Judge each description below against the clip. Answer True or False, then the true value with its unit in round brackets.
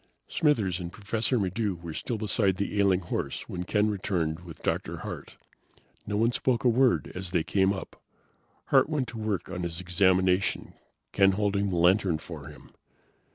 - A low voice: True (95 Hz)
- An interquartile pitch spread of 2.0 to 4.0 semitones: True (3.3 semitones)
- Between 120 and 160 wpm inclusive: False (170 wpm)